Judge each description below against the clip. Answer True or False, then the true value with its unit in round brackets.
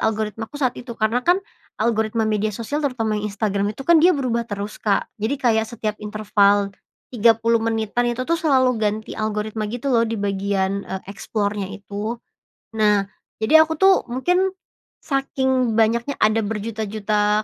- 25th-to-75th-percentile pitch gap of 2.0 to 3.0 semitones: True (2.7 semitones)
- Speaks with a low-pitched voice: False (220 Hz)